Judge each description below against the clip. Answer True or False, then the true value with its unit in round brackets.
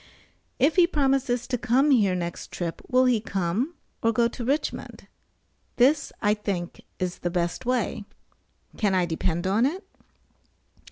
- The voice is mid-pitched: False (230 Hz)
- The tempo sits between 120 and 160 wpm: True (150 wpm)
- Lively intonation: True (6.2 semitones)